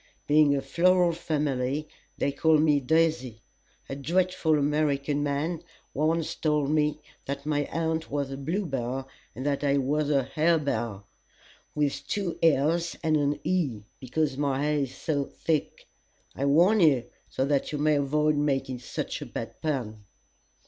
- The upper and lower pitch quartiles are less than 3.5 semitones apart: Yes, narrow, 2.4 semitones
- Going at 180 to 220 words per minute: No, average, 150 wpm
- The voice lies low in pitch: No, medium, 145 Hz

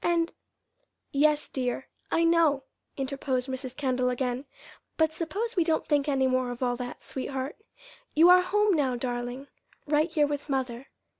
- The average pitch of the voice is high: Yes, very high, 275 Hz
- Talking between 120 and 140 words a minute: No, average, 160 wpm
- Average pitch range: Yes, average, 3.9 semitones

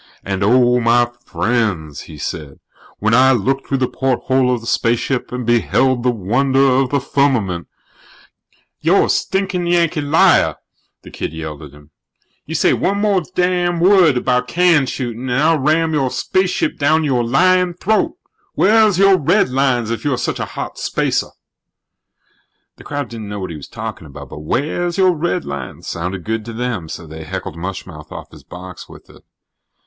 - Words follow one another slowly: No, average, 175 wpm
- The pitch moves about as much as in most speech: No, wide, 7.1 semitones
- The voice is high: No, low, 130 Hz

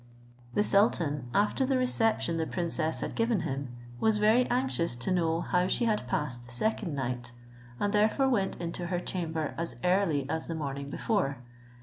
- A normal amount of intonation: No, wide, 6.3 semitones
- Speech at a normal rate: Yes, average, 170 wpm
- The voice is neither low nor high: Yes, medium, 175 Hz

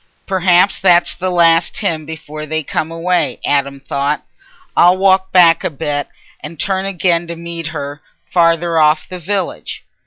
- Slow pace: No, average, 155 wpm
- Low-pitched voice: No, medium, 170 Hz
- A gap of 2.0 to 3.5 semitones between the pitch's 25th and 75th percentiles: Yes, average, 2.9 semitones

